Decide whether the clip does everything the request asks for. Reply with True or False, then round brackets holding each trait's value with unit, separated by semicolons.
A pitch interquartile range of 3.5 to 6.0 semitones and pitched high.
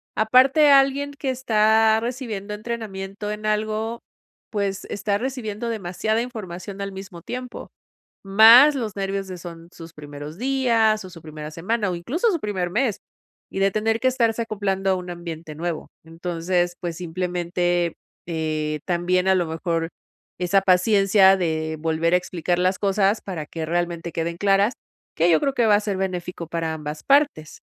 True (4.2 semitones; 195 Hz)